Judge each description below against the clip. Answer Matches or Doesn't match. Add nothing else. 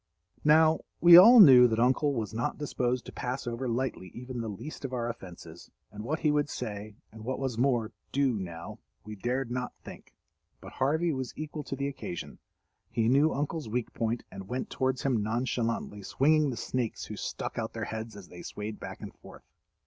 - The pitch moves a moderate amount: Matches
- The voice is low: Matches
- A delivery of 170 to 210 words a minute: Matches